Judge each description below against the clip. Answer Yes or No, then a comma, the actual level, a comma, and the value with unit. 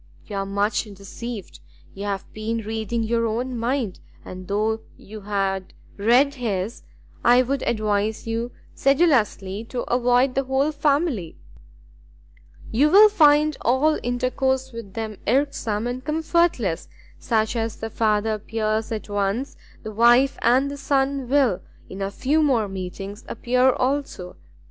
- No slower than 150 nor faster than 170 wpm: No, average, 140 wpm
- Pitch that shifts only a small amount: No, average, 4.2 semitones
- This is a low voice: No, high, 230 Hz